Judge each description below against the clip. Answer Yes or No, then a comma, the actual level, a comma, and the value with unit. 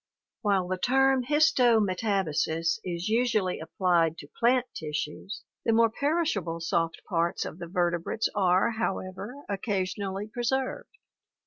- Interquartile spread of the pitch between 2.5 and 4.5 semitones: No, wide, 5.6 semitones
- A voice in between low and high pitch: No, high, 200 Hz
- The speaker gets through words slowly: Yes, slow, 130 wpm